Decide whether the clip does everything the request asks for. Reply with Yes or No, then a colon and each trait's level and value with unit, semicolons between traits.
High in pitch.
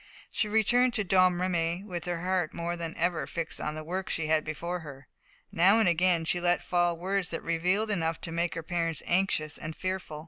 No: medium, 175 Hz